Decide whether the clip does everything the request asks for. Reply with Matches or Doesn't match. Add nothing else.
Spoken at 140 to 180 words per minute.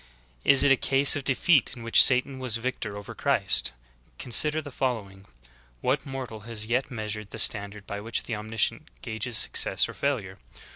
Matches